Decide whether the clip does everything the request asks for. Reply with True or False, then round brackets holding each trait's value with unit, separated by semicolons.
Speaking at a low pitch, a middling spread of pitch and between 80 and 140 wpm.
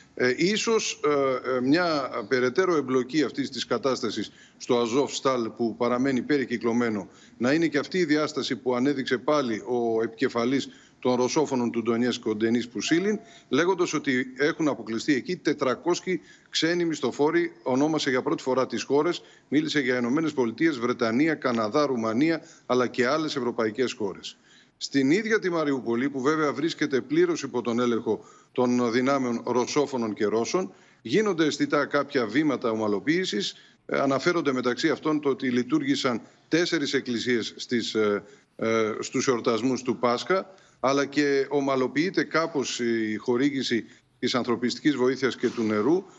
True (130 Hz; 3.9 semitones; 135 wpm)